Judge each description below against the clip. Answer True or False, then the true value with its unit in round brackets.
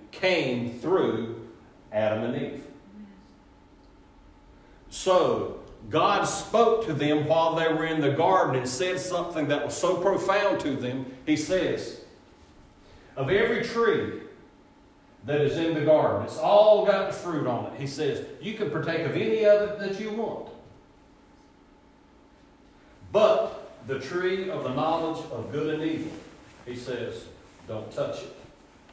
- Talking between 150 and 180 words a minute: False (140 wpm)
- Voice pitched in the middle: True (165 Hz)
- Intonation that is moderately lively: False (7.0 semitones)